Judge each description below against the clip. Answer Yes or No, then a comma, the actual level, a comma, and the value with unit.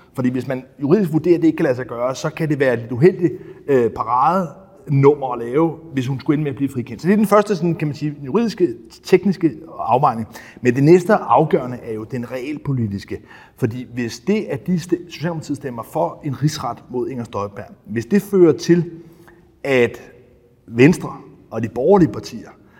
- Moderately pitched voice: Yes, medium, 145 Hz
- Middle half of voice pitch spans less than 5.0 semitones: No, wide, 5.5 semitones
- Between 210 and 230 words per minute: No, average, 195 wpm